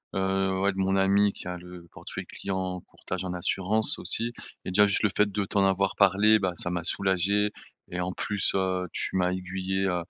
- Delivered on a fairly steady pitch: Yes, narrow, 1.5 semitones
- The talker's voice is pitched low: Yes, very low, 95 Hz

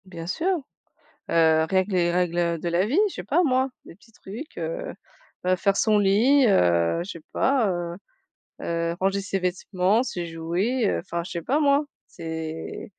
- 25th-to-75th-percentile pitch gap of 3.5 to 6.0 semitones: Yes, average, 5.2 semitones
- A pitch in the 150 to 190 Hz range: Yes, medium, 185 Hz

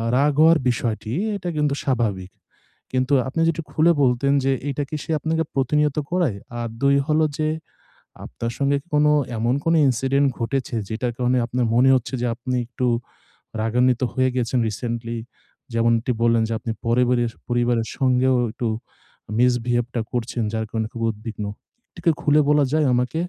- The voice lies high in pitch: No, low, 125 Hz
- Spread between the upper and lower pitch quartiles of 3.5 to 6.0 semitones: No, average, 3.1 semitones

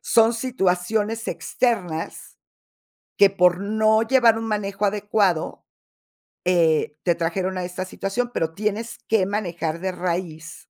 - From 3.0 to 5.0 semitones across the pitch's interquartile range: Yes, average, 3.8 semitones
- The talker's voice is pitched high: Yes, high, 195 Hz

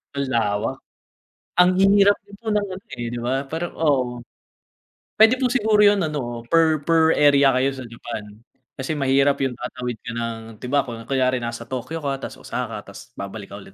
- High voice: No, low, 135 Hz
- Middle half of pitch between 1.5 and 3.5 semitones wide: No, average, 5.2 semitones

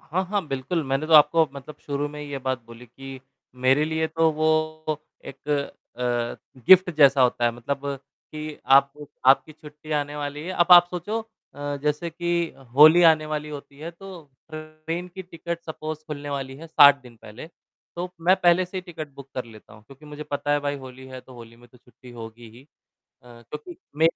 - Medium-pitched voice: Yes, medium, 150 Hz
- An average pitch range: Yes, average, 3.3 semitones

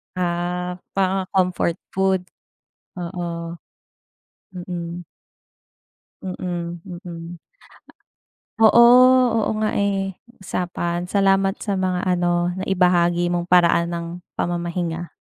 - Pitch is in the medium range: Yes, medium, 180 Hz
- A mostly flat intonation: Yes, narrow, 1.6 semitones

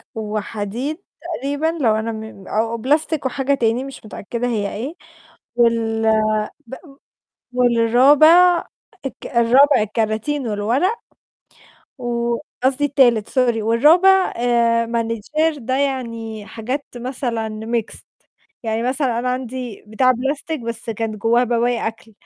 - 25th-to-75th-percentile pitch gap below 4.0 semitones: Yes, average, 3.3 semitones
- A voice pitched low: No, high, 240 Hz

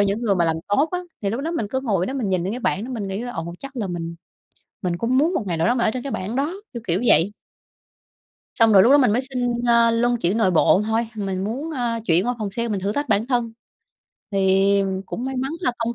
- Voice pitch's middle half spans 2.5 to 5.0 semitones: Yes, average, 4.3 semitones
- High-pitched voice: Yes, high, 225 Hz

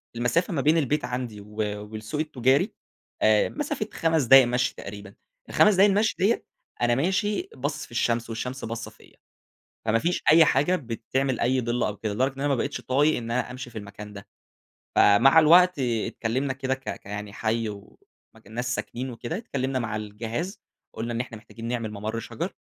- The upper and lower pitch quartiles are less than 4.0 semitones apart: No, average, 4.3 semitones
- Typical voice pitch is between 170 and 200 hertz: No, low, 125 Hz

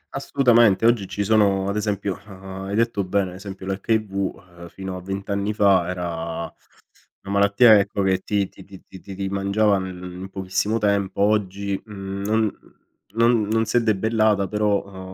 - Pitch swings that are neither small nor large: No, narrow, 1.8 semitones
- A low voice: Yes, low, 100 Hz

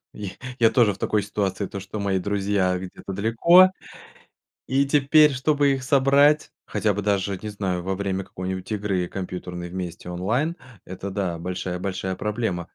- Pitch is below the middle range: Yes, low, 100 Hz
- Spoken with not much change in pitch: No, average, 4.1 semitones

